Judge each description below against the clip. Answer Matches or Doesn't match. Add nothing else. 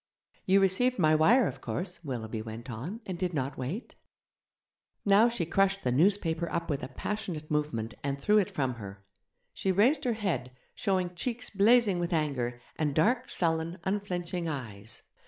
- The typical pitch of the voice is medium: Matches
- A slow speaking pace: Doesn't match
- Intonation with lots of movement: Matches